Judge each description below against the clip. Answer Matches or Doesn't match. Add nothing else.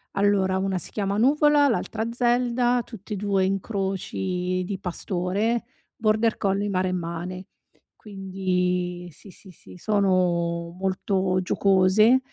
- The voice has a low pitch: Doesn't match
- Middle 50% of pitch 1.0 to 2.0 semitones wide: Doesn't match